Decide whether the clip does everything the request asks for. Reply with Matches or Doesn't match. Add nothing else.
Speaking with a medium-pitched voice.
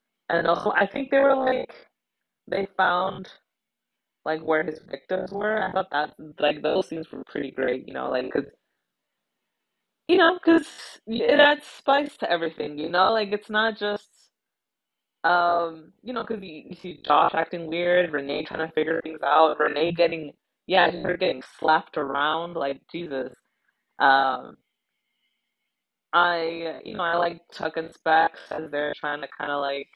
Matches